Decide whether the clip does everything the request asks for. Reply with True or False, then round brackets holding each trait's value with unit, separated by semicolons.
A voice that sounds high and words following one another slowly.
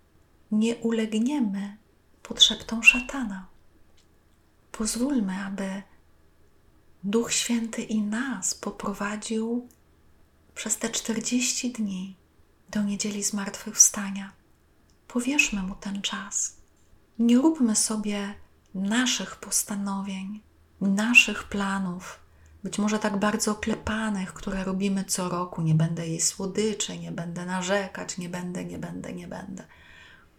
True (200 Hz; 100 wpm)